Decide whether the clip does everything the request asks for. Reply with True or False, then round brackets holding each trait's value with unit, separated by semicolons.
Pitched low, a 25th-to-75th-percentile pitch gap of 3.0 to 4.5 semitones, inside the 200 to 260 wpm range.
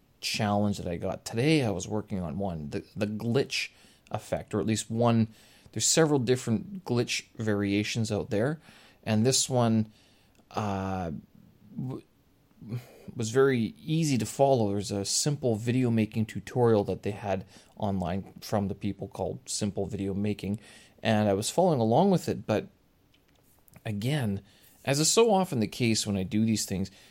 False (110 Hz; 3.5 semitones; 160 wpm)